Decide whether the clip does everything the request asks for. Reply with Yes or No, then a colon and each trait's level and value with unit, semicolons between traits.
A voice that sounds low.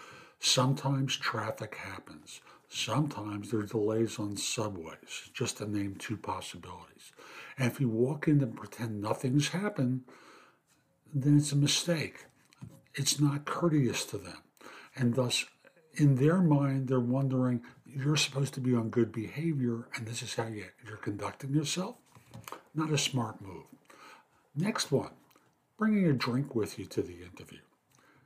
Yes: low, 130 Hz